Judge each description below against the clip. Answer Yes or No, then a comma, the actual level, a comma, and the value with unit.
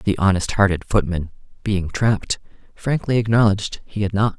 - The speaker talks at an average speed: Yes, average, 150 wpm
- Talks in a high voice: No, low, 100 Hz